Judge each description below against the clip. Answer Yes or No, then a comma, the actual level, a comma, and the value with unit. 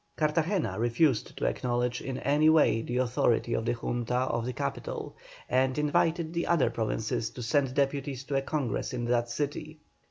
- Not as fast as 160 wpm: No, average, 170 wpm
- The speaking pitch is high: No, low, 130 Hz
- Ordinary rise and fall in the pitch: Yes, average, 3.8 semitones